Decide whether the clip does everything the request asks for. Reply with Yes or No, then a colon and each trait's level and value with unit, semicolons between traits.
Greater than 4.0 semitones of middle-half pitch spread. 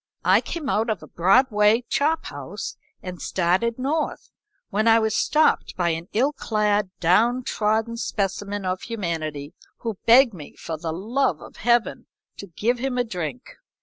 Yes: average, 4.9 semitones